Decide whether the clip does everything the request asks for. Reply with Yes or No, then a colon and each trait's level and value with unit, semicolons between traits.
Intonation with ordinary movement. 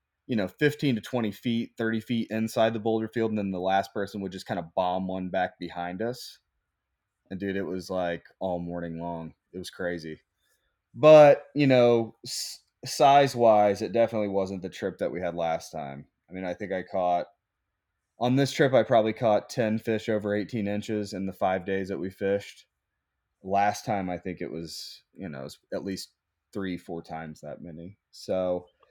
Yes: average, 3.9 semitones